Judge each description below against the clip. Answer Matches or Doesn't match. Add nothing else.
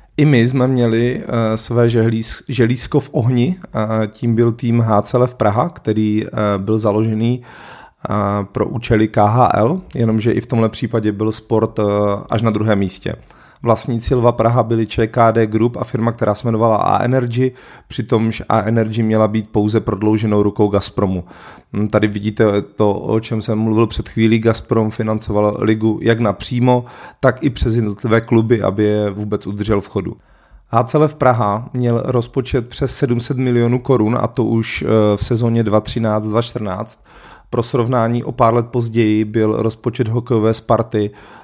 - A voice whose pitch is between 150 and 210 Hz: Doesn't match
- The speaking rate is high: Doesn't match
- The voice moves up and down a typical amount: Doesn't match